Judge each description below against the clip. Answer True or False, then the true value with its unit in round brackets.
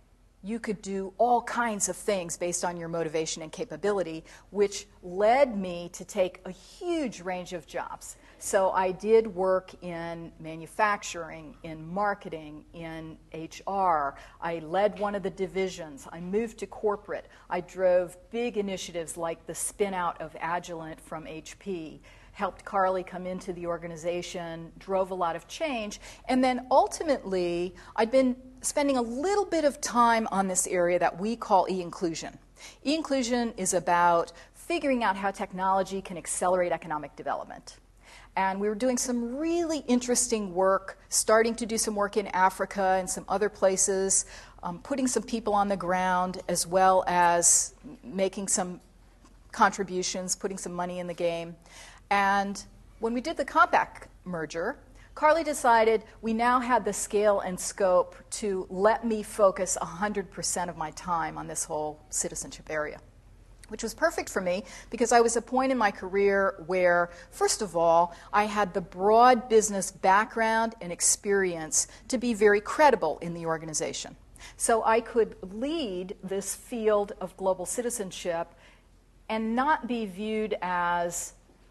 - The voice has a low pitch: False (190 Hz)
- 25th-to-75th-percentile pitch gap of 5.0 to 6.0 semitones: False (4.3 semitones)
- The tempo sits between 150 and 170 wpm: True (155 wpm)